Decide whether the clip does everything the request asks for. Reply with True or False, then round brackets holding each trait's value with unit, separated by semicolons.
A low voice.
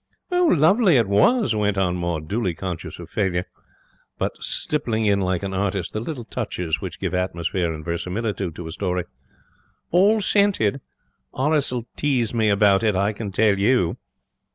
True (100 Hz)